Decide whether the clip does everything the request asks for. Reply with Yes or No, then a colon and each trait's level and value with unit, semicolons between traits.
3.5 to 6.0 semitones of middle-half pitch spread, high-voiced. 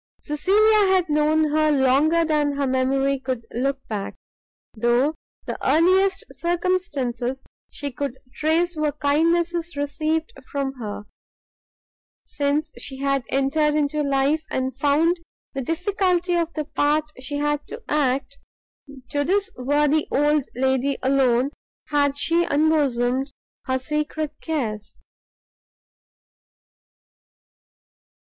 No: average, 2.9 semitones; very high, 290 Hz